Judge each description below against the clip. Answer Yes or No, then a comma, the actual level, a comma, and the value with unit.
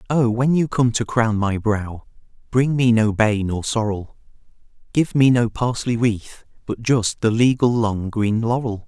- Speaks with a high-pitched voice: No, low, 115 Hz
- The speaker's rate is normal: Yes, average, 175 wpm